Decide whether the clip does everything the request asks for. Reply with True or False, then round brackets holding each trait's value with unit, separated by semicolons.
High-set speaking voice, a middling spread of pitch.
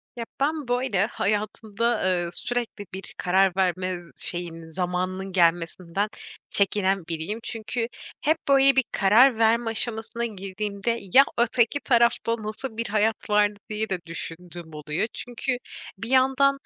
True (210 Hz; 4.3 semitones)